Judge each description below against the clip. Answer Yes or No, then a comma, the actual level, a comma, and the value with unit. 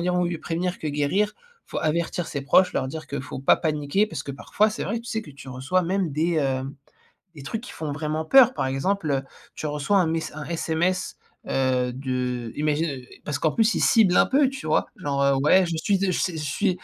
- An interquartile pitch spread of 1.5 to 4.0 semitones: No, average, 4.8 semitones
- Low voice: No, medium, 160 Hz